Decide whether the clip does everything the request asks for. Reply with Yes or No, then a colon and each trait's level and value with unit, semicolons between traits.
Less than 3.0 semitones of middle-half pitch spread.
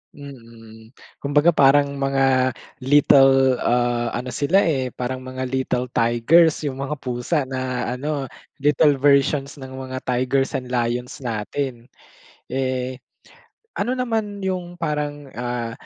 Yes: narrow, 2.6 semitones